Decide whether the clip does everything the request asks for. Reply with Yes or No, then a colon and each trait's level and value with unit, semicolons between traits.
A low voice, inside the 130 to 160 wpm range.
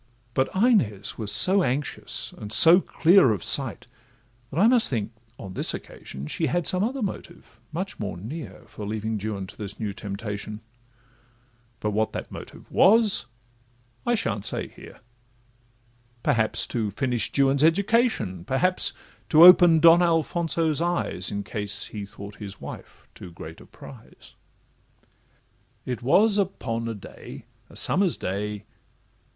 Yes: low, 125 Hz; average, 145 wpm